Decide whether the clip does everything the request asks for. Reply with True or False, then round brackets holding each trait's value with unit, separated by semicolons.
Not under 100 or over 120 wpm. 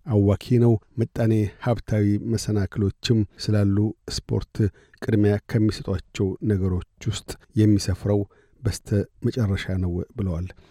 False (90 wpm)